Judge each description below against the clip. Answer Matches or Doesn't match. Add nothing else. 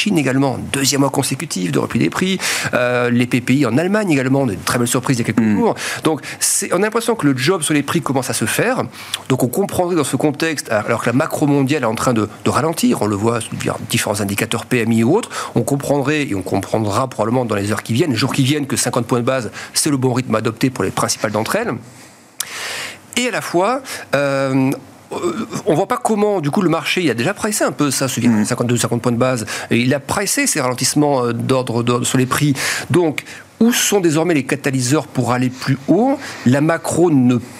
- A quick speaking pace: Matches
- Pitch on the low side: Matches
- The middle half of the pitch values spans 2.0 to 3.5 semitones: Doesn't match